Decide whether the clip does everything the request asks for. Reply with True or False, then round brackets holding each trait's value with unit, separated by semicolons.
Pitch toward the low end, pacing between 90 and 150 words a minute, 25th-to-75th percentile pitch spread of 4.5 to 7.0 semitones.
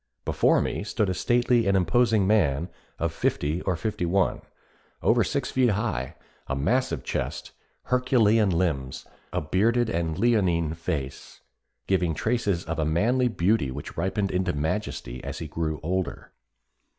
True (95 Hz; 145 wpm; 5.4 semitones)